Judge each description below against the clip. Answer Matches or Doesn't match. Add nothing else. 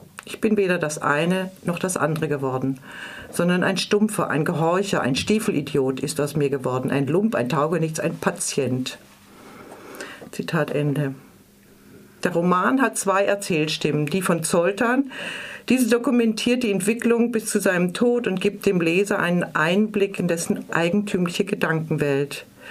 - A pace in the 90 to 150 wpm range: Matches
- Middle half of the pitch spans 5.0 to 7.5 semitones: Matches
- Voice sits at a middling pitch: Matches